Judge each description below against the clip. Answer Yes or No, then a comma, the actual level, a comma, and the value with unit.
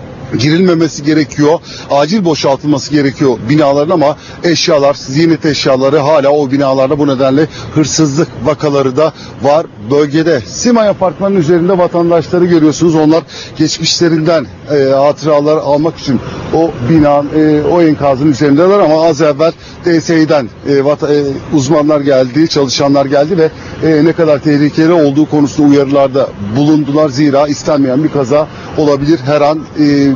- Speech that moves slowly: No, average, 130 wpm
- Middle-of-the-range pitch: Yes, medium, 150 Hz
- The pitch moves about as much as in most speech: No, narrow, 2.3 semitones